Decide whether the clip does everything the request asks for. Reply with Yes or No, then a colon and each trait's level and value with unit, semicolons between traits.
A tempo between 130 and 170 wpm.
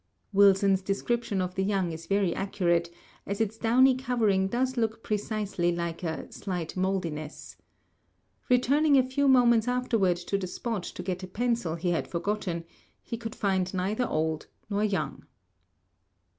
Yes: average, 150 wpm